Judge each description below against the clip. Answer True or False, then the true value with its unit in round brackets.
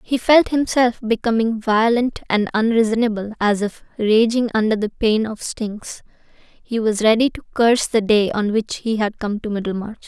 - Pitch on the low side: False (220 Hz)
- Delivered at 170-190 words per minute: True (175 wpm)